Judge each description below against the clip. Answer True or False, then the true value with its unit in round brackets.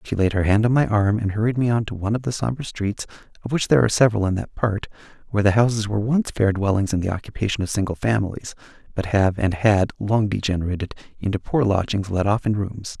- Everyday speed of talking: False (235 wpm)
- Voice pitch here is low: True (105 Hz)